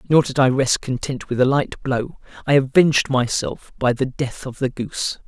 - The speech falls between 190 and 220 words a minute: Yes, fast, 205 wpm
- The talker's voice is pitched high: No, low, 135 Hz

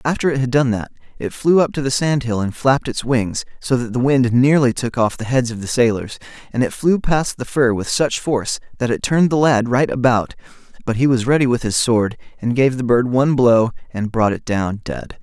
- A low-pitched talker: Yes, low, 125 Hz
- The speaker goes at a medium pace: No, fast, 240 wpm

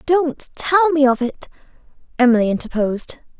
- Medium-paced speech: No, slow, 125 wpm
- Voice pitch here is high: Yes, very high, 275 Hz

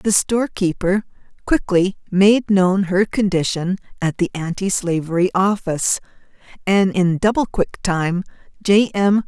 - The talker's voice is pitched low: No, high, 190 Hz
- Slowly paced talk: Yes, slow, 130 wpm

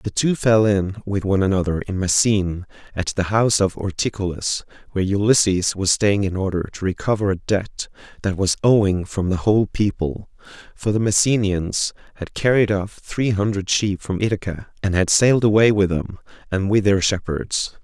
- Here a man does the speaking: Yes, male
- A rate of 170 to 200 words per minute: Yes, average, 175 wpm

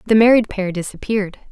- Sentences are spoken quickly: No, average, 160 wpm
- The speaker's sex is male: No, female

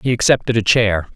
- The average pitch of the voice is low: Yes, low, 110 Hz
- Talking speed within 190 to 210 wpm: Yes, fast, 205 wpm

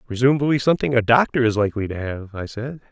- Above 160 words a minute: Yes, fast, 205 wpm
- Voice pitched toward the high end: No, low, 120 Hz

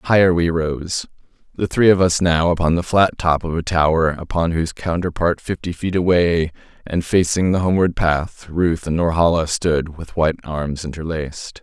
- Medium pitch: No, very low, 85 Hz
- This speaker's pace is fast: No, average, 175 wpm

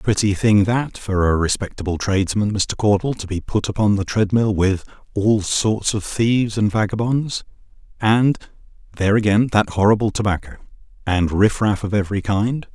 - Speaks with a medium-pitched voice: No, low, 105 Hz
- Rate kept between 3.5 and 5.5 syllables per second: Yes, 5.0 syllables/s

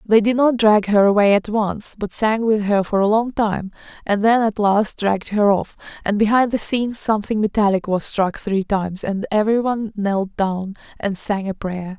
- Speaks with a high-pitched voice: Yes, high, 210 Hz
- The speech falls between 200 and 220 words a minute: Yes, fast, 205 wpm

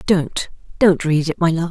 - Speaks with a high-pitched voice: No, medium, 165 Hz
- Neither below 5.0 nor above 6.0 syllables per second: No, 4.7 syllables/s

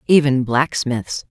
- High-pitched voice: No, low, 135 Hz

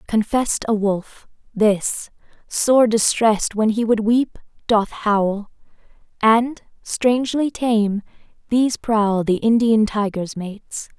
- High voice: Yes, high, 220 Hz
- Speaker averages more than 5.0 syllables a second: No, 3.7 syllables/s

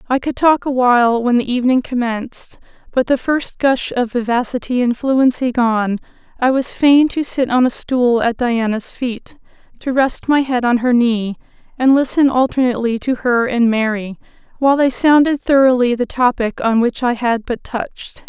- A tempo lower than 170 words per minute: No, average, 180 wpm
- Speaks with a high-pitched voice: Yes, very high, 250 Hz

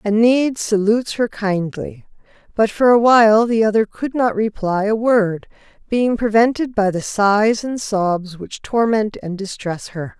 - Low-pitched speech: No, high, 215 Hz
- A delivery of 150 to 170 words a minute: Yes, average, 160 wpm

